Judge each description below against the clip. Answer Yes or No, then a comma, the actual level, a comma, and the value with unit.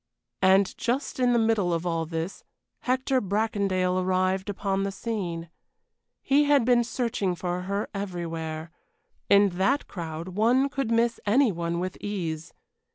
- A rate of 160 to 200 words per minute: No, average, 145 wpm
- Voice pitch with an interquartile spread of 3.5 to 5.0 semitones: Yes, average, 4.7 semitones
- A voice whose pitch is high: Yes, high, 195 Hz